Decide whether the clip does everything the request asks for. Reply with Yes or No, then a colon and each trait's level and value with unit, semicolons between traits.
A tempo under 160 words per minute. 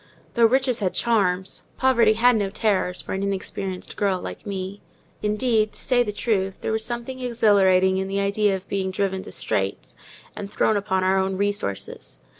No: average, 180 wpm